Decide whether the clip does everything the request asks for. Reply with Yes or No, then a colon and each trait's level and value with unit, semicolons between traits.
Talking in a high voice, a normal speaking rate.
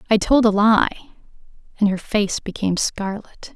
Yes: high, 210 Hz; average, 150 wpm